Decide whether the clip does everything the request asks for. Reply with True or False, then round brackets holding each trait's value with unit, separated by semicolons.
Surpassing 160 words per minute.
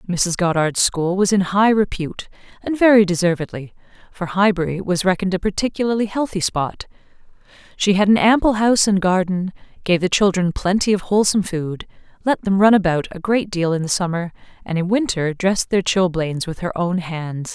True (175 wpm)